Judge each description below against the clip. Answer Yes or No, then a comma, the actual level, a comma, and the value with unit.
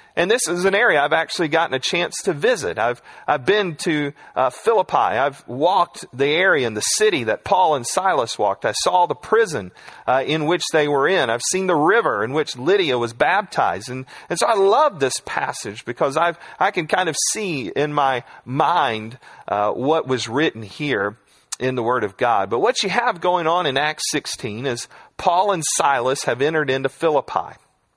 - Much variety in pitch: Yes, wide, 7.3 semitones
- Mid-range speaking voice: Yes, medium, 160 Hz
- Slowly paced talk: No, average, 200 wpm